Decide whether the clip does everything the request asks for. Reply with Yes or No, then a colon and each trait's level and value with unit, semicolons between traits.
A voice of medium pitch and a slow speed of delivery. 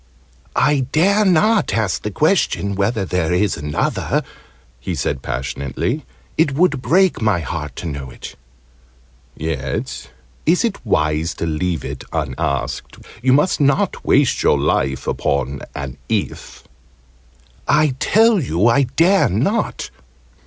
No: low, 100 Hz; slow, 130 wpm